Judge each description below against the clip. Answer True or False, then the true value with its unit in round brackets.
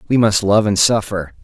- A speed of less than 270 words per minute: True (210 wpm)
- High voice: False (105 Hz)